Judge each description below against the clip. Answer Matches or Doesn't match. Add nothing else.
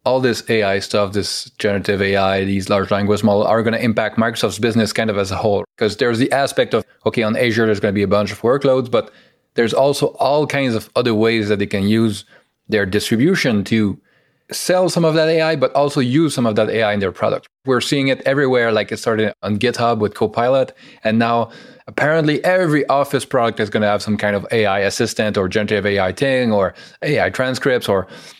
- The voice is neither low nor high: Doesn't match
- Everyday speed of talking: Doesn't match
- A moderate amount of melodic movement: Matches